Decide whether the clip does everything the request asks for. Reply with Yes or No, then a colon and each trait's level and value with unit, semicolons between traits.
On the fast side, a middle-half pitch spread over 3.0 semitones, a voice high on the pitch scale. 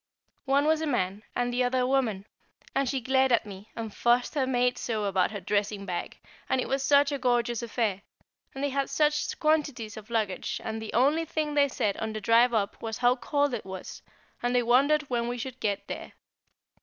Yes: fast, 215 wpm; average, 3.9 semitones; high, 245 Hz